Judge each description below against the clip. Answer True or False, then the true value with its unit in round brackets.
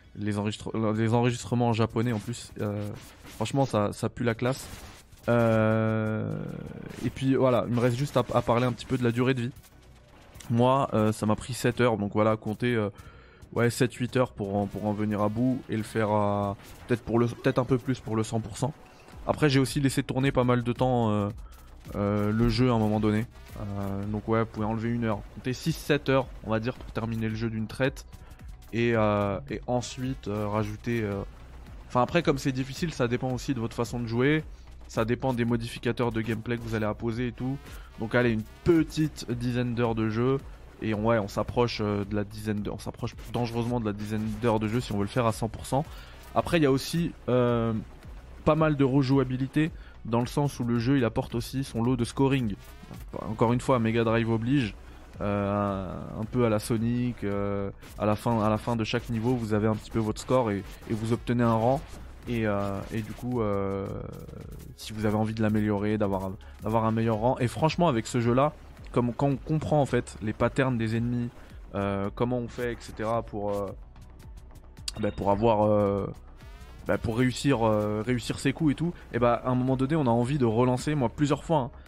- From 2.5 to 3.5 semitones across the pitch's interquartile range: True (3.1 semitones)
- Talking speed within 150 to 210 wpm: False (220 wpm)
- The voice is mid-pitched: False (115 Hz)